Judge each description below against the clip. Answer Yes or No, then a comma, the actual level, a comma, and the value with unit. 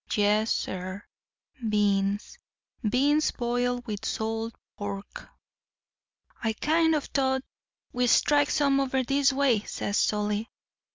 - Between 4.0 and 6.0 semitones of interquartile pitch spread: Yes, average, 4.7 semitones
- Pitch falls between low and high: No, high, 235 Hz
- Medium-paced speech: No, slow, 105 wpm